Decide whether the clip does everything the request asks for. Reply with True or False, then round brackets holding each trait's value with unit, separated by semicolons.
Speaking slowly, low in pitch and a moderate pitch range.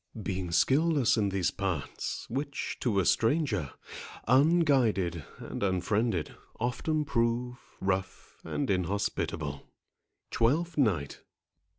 False (95 wpm; 110 Hz; 6.6 semitones)